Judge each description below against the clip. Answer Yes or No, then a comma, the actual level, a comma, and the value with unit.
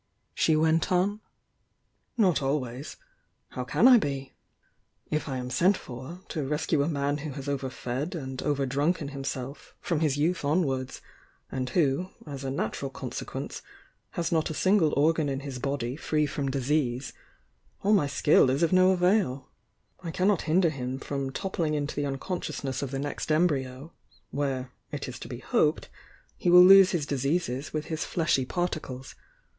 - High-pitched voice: No, medium, 145 Hz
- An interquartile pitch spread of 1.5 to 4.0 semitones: Yes, average, 3.7 semitones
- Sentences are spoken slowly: No, average, 175 wpm